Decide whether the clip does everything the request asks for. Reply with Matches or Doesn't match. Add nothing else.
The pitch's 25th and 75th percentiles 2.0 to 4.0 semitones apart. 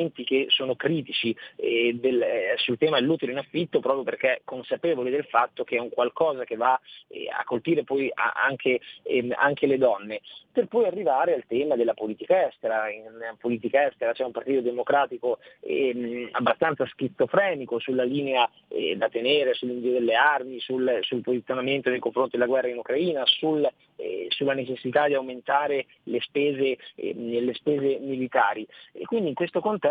Doesn't match